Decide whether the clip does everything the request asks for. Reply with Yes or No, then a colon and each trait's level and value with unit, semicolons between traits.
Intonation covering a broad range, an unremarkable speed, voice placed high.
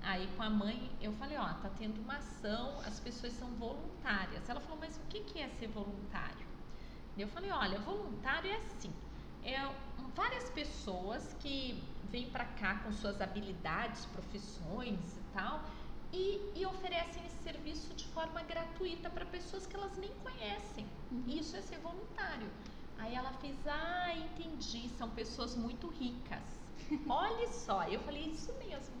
Yes: wide, 7.6 semitones; average, 160 wpm; very high, 255 Hz